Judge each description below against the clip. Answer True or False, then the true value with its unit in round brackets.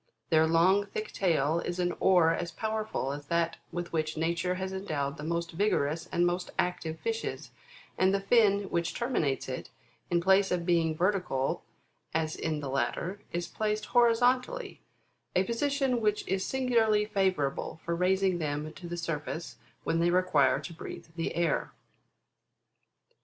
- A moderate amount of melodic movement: True (3.7 semitones)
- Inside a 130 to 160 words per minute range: True (155 wpm)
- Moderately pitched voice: True (175 Hz)